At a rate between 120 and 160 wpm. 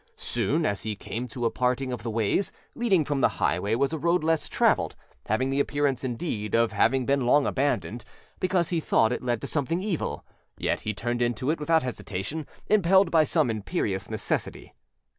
No: average, 185 wpm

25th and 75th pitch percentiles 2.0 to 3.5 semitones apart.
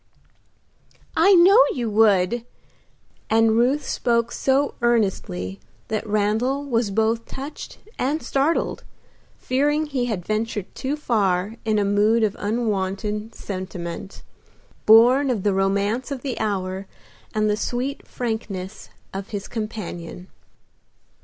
No: average, 4.0 semitones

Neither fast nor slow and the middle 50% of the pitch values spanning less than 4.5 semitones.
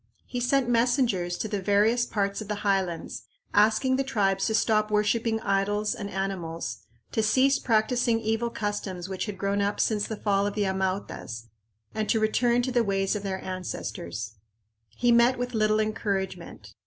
Yes: average, 170 wpm; average, 3.0 semitones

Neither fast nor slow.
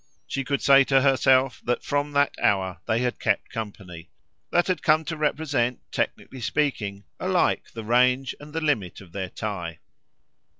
Yes: average, 165 wpm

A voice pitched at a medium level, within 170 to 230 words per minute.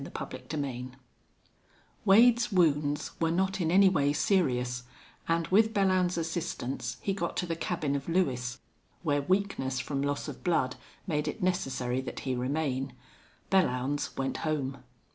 No: medium, 155 Hz; average, 145 wpm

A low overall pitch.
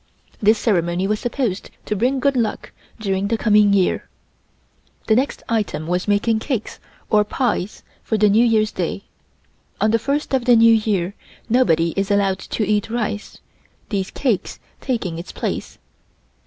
No: high, 215 Hz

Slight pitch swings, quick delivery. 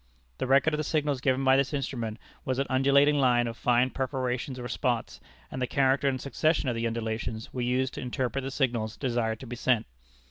Yes: narrow, 2.1 semitones; fast, 210 wpm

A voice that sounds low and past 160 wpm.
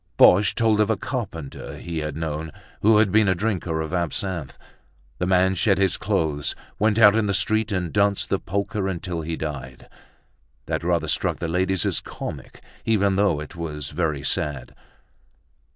Yes: very low, 95 Hz; average, 170 wpm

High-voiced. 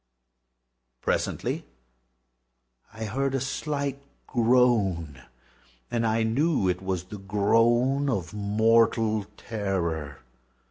No: low, 110 Hz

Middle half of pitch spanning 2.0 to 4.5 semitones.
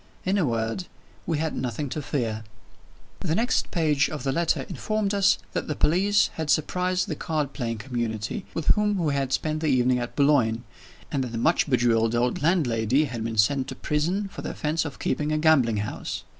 No: average, 5.2 semitones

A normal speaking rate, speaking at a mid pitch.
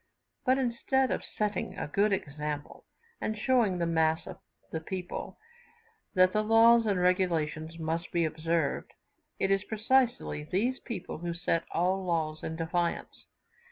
Yes: average, 145 wpm; medium, 180 Hz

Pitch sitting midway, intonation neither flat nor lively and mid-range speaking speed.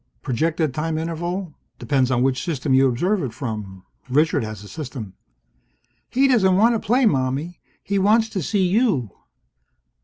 No: medium, 155 Hz; wide, 7.0 semitones; average, 155 wpm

